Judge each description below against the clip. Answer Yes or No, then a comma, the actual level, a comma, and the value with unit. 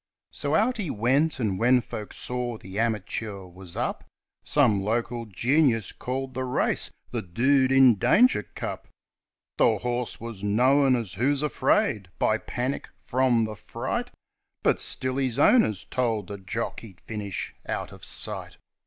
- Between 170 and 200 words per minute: No, average, 155 wpm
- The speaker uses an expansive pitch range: No, average, 3.8 semitones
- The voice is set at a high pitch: No, low, 120 Hz